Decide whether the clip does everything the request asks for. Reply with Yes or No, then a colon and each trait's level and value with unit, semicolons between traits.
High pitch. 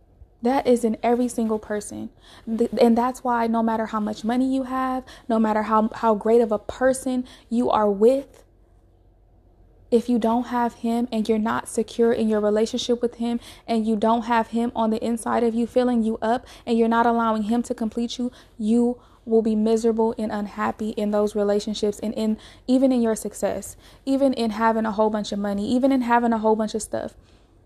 Yes: high, 230 Hz